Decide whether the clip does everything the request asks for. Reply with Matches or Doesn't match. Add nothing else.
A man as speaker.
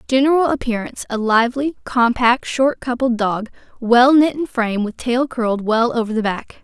Doesn't match